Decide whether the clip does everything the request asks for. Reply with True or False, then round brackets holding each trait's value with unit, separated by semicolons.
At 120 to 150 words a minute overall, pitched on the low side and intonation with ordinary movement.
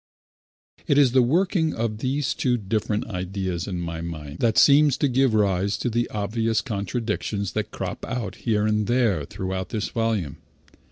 False (165 wpm; 110 Hz; 4.3 semitones)